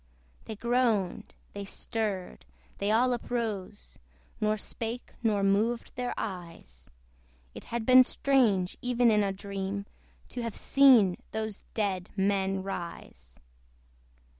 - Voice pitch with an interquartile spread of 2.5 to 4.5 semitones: Yes, average, 3.5 semitones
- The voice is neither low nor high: No, high, 210 Hz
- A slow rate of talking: Yes, slow, 115 wpm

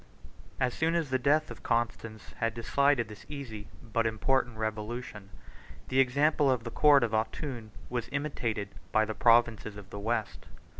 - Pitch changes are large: No, average, 3.7 semitones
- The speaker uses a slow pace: No, average, 165 wpm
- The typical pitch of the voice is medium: No, low, 120 Hz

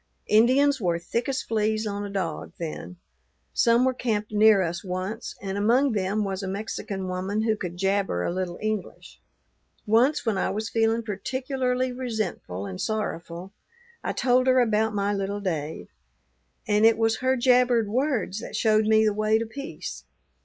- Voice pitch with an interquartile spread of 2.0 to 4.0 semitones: Yes, average, 3.4 semitones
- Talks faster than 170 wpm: No, average, 165 wpm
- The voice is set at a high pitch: Yes, high, 215 Hz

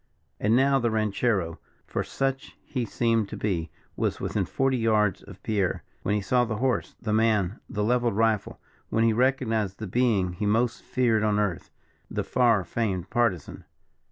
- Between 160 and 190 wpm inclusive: Yes, average, 170 wpm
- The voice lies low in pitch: Yes, low, 110 Hz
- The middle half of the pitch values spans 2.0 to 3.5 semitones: Yes, average, 2.9 semitones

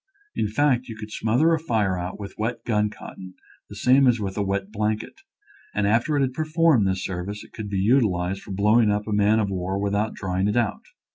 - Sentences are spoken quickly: Yes, fast, 225 wpm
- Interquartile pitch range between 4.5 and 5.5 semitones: No, average, 3.1 semitones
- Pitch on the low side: Yes, low, 105 Hz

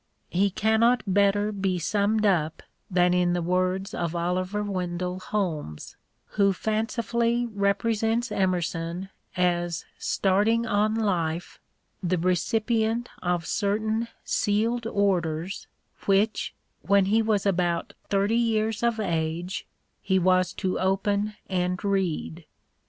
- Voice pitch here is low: No, high, 195 Hz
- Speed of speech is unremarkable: No, slow, 115 wpm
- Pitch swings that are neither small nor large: Yes, average, 3.2 semitones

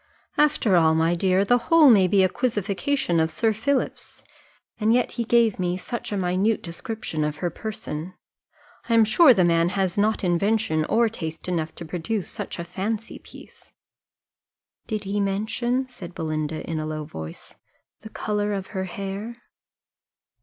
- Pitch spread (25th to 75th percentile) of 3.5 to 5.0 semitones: Yes, average, 4.7 semitones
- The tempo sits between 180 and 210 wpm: No, average, 160 wpm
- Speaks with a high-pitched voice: Yes, high, 195 Hz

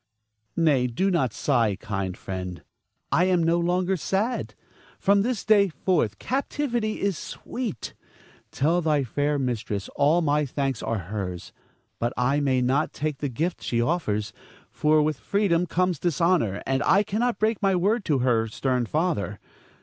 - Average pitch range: No, wide, 7.1 semitones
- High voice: No, medium, 150 Hz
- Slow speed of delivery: No, average, 155 wpm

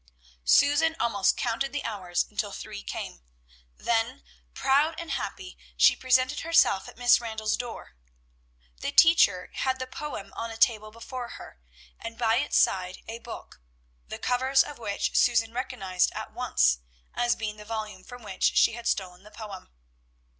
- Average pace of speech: Yes, average, 160 wpm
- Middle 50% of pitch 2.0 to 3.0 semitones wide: No, average, 3.8 semitones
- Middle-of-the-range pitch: No, high, 230 Hz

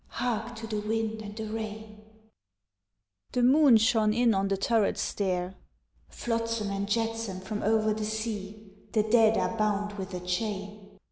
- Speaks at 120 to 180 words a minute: Yes, average, 155 wpm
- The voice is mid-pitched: No, high, 215 Hz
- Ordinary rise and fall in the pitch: No, narrow, 1.7 semitones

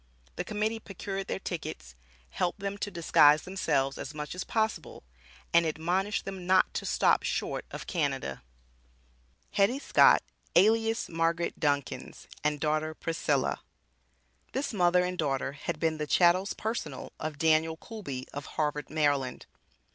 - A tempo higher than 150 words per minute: No, average, 140 wpm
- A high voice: No, medium, 165 Hz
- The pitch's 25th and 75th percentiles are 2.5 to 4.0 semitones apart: No, average, 4.5 semitones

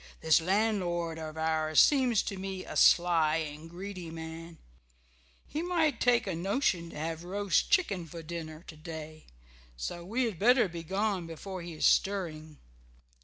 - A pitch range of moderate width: Yes, average, 3.8 semitones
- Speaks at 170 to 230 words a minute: No, average, 160 wpm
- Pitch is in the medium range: Yes, medium, 170 Hz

